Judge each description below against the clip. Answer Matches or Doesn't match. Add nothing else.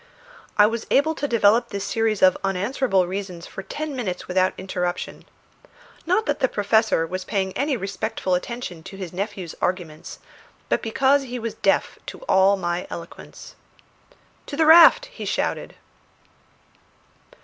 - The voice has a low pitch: Doesn't match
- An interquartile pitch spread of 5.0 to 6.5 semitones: Matches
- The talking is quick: Doesn't match